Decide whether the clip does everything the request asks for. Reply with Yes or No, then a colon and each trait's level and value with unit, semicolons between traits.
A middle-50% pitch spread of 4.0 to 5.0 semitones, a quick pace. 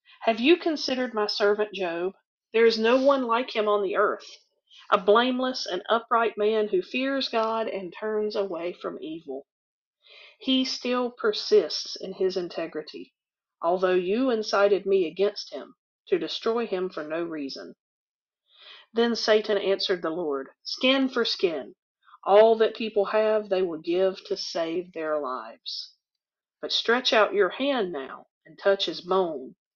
No: average, 4.7 semitones; average, 150 wpm